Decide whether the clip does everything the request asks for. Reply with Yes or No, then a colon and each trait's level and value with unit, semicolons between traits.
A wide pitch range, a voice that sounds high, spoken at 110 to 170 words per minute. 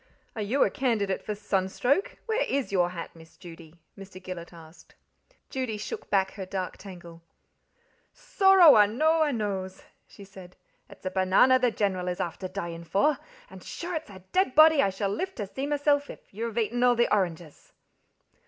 No: wide, 6.1 semitones; high, 200 Hz; average, 180 wpm